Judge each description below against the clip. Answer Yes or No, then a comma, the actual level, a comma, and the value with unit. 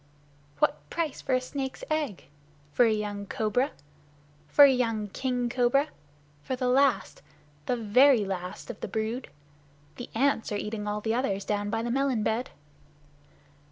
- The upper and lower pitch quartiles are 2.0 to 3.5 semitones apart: No, average, 3.9 semitones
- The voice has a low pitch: No, high, 235 Hz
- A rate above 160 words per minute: No, average, 155 wpm